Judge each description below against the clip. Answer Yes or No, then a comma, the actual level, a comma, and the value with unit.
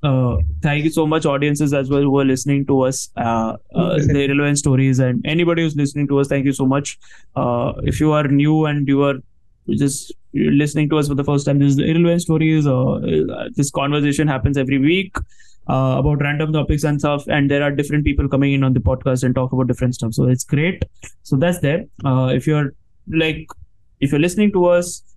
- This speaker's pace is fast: Yes, fast, 215 wpm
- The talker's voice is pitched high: No, medium, 140 Hz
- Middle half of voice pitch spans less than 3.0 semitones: Yes, narrow, 2.4 semitones